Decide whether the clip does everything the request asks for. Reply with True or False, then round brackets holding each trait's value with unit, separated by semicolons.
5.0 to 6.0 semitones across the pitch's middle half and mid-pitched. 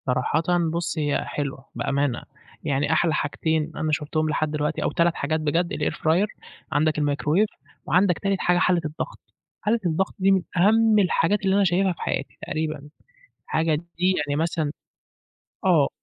False (3.3 semitones; 160 Hz)